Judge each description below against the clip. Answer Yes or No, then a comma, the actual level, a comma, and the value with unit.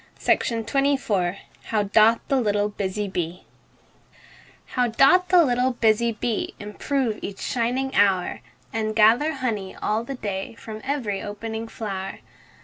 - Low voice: No, high, 225 Hz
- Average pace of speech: No, slow, 130 wpm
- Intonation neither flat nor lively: Yes, average, 3.5 semitones